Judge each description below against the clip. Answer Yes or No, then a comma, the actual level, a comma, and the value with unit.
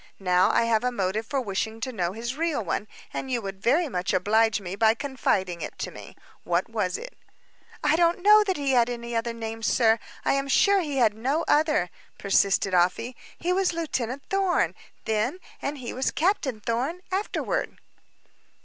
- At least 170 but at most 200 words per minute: Yes, average, 185 wpm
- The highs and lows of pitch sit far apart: Yes, wide, 5.8 semitones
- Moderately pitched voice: No, high, 240 Hz